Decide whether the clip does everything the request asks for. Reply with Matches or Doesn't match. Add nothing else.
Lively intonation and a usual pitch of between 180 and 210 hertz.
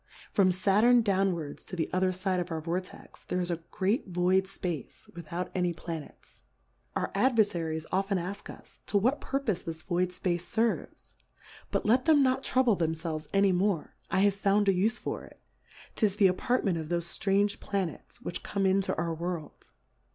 Doesn't match